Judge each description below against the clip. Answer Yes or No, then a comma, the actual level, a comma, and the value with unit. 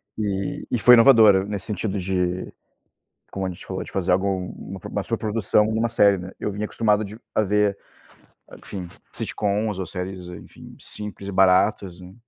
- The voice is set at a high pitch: No, low, 100 Hz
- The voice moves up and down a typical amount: No, narrow, 2.2 semitones